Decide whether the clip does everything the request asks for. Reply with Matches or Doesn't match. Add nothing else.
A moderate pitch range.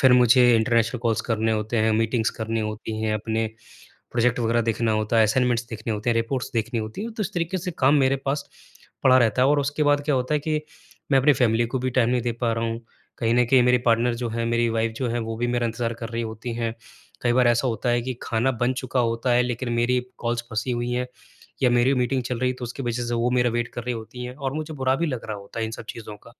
Doesn't match